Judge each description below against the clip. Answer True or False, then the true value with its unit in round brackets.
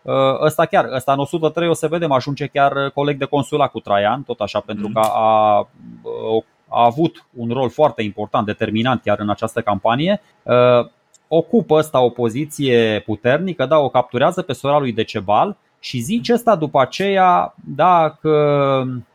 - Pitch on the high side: False (135 Hz)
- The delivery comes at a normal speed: True (155 wpm)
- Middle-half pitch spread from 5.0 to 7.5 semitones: True (5.4 semitones)